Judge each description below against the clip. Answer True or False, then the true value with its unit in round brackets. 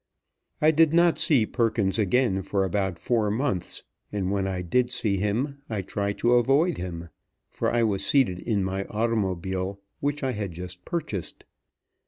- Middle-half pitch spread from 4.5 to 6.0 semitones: True (4.8 semitones)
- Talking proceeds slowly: False (165 wpm)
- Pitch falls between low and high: False (105 Hz)